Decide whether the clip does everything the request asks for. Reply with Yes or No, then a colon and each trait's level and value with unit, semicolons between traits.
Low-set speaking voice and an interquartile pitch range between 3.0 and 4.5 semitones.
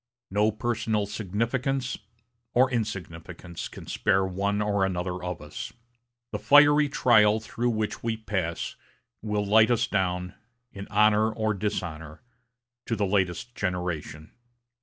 Yes: low, 105 Hz; average, 3.6 semitones